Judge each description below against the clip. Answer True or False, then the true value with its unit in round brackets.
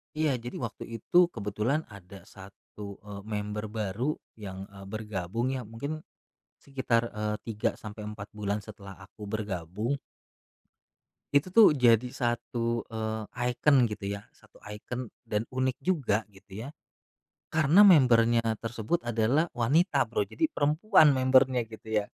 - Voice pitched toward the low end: True (115 Hz)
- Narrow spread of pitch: False (3.8 semitones)